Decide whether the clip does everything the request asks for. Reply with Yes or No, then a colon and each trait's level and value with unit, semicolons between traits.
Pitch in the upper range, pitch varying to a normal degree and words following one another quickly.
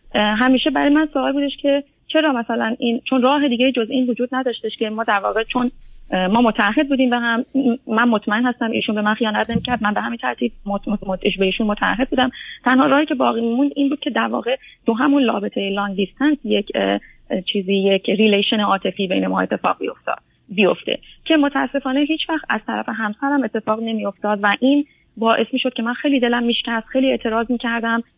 Yes: high, 235 Hz; average, 4.2 semitones; fast, 200 wpm